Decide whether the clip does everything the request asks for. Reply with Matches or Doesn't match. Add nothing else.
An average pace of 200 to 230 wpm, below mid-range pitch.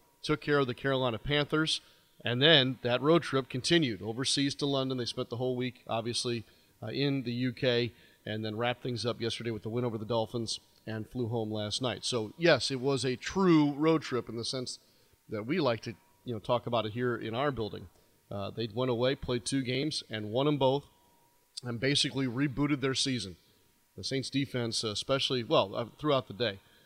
Matches